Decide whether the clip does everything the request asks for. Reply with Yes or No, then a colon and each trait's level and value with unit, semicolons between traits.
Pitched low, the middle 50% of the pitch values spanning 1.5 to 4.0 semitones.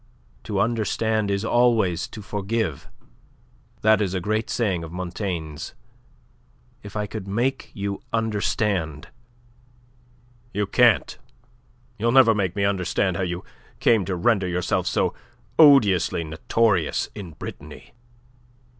Yes: low, 100 Hz; average, 3.5 semitones